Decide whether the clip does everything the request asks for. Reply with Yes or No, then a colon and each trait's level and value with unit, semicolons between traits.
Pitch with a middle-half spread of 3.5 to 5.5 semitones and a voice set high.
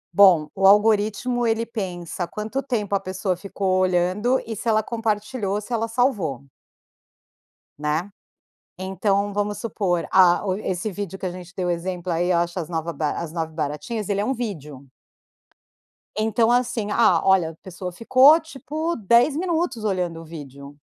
Yes: average, 4.3 semitones; high, 195 Hz